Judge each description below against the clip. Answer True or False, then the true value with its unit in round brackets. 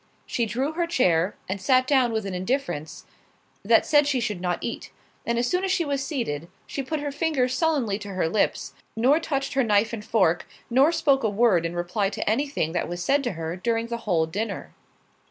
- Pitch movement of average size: False (6.7 semitones)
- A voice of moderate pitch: False (230 Hz)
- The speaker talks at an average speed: False (215 wpm)